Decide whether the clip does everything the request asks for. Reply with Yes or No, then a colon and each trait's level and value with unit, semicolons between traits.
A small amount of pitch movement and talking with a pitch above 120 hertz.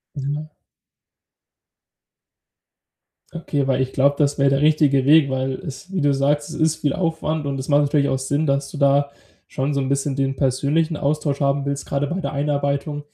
Yes: narrow, 1.5 semitones; medium, 140 Hz